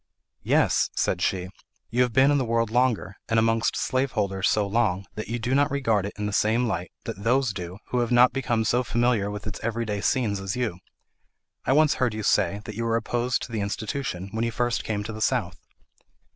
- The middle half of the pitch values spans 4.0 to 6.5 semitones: No, average, 3.2 semitones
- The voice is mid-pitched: No, low, 115 Hz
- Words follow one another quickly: Yes, fast, 220 wpm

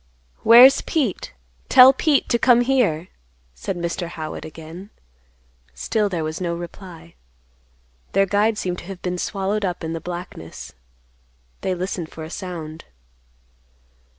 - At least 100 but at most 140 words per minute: Yes, slow, 135 wpm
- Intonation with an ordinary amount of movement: Yes, average, 4.0 semitones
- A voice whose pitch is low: No, medium, 180 Hz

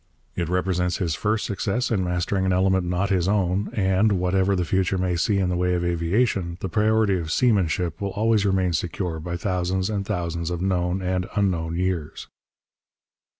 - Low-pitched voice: Yes, very low, 95 Hz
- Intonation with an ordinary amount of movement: No, narrow, 2.0 semitones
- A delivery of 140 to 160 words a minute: No, average, 180 wpm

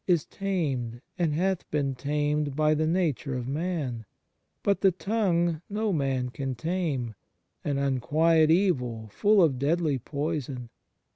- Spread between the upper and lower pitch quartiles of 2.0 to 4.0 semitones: No, average, 4.5 semitones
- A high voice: No, medium, 150 Hz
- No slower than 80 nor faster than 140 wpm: Yes, slow, 135 wpm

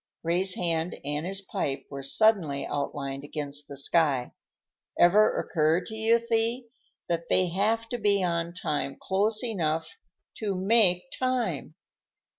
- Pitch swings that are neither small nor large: No, wide, 6.0 semitones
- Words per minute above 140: No, slow, 135 wpm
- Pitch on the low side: No, medium, 175 Hz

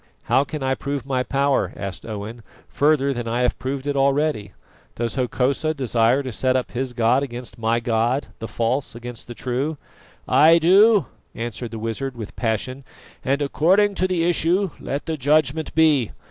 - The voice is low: Yes, low, 130 Hz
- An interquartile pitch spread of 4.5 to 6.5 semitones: No, average, 3.9 semitones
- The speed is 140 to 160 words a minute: No, average, 175 wpm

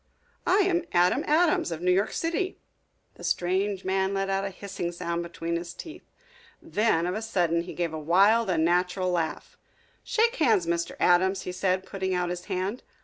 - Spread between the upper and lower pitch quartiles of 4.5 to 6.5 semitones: No, average, 2.9 semitones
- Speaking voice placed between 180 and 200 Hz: Yes, medium, 185 Hz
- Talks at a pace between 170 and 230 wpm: Yes, average, 180 wpm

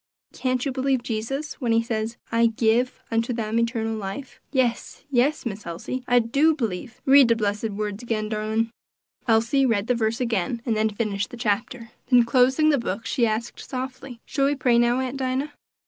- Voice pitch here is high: Yes, high, 235 Hz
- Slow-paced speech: No, average, 185 wpm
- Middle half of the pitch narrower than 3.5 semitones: Yes, average, 2.7 semitones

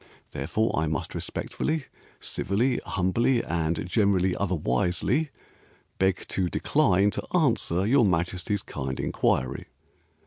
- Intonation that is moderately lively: Yes, average, 5.0 semitones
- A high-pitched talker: No, very low, 95 Hz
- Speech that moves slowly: Yes, slow, 105 wpm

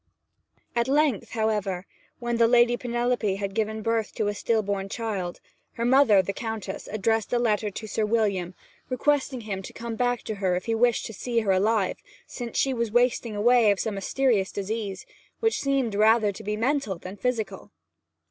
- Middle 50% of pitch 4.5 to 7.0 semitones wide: No, average, 3.1 semitones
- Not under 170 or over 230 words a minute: Yes, average, 185 wpm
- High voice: Yes, high, 220 Hz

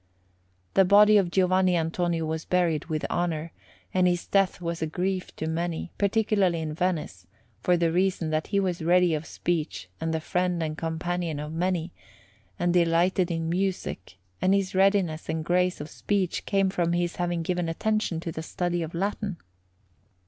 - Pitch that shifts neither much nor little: No, narrow, 2.3 semitones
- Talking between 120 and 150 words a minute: No, average, 170 wpm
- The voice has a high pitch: No, medium, 175 Hz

